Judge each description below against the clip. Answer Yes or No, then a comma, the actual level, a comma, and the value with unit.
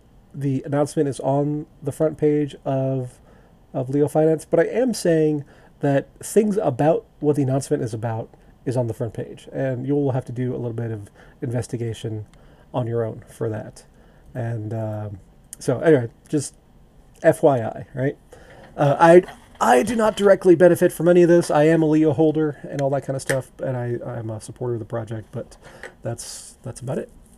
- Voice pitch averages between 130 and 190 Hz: Yes, medium, 140 Hz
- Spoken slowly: No, average, 190 wpm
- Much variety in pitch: No, average, 4.5 semitones